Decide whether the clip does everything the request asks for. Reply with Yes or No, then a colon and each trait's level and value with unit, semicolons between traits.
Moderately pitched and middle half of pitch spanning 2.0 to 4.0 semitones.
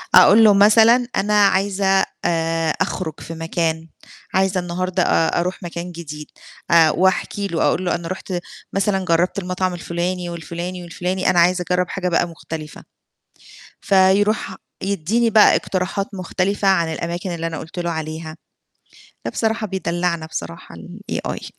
Yes: medium, 180 Hz; narrow, 2.5 semitones